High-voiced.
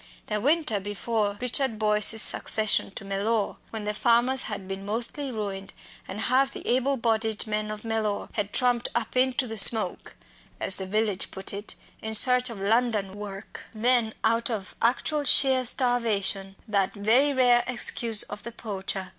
Yes: high, 220 Hz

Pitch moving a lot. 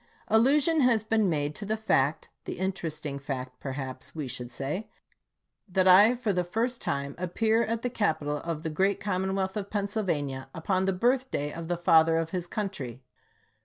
Yes: wide, 6.3 semitones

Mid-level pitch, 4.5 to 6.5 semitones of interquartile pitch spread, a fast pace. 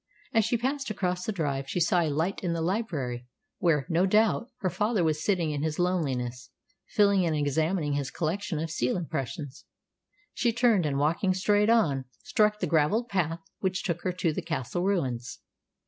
No: medium, 170 Hz; average, 5.2 semitones; average, 180 wpm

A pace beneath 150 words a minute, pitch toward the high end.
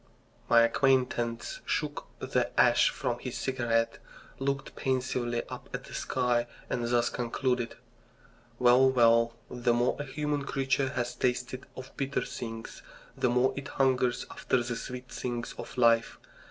No: average, 140 wpm; low, 125 Hz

